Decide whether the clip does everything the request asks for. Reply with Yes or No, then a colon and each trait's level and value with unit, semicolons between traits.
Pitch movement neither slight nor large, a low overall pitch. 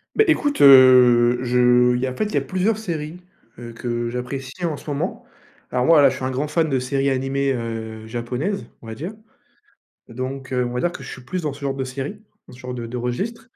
Yes: average, 3.5 semitones; low, 130 Hz